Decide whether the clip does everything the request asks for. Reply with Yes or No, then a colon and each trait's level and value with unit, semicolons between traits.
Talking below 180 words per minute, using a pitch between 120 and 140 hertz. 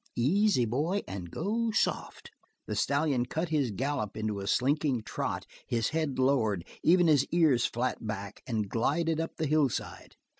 Yes: average, 155 wpm; low, 135 Hz